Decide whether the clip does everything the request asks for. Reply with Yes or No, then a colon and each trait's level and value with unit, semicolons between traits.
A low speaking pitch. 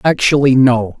Yes: low, 130 Hz